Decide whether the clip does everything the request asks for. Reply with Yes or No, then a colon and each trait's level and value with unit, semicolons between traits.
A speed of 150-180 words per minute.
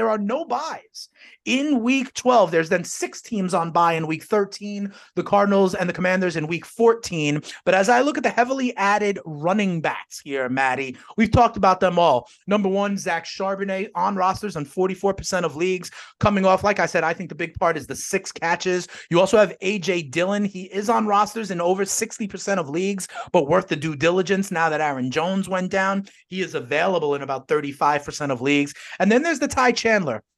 No: fast, 205 wpm